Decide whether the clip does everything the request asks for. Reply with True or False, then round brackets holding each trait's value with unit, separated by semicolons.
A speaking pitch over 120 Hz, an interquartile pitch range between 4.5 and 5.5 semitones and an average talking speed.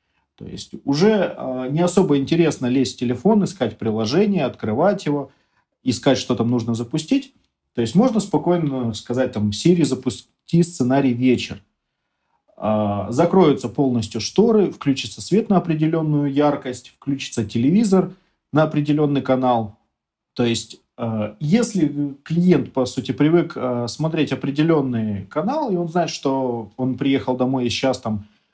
True (135 Hz; 5.2 semitones; 135 wpm)